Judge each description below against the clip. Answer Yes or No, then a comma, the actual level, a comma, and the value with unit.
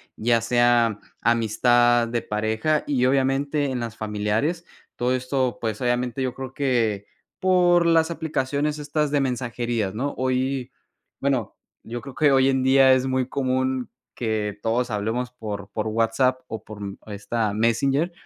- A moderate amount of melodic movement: Yes, average, 3.1 semitones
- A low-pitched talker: Yes, low, 125 Hz